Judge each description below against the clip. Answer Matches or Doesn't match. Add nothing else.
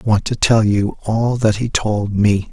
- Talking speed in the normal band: Doesn't match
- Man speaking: Matches